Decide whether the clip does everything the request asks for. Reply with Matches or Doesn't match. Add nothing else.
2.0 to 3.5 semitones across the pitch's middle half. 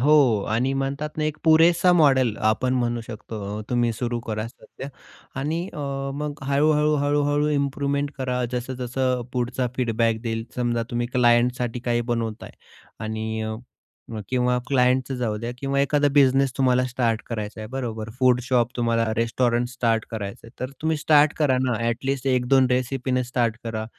Matches